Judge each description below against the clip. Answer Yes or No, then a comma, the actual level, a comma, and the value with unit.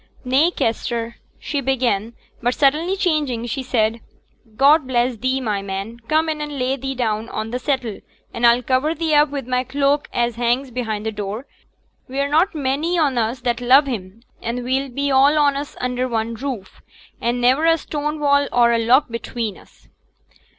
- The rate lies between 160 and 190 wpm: Yes, average, 185 wpm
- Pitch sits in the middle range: No, very high, 255 Hz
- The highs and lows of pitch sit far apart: No, average, 3.4 semitones